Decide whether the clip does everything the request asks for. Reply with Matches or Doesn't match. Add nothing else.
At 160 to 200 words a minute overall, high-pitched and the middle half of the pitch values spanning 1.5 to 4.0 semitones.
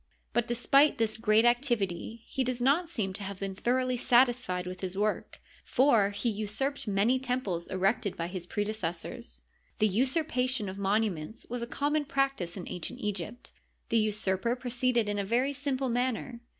Doesn't match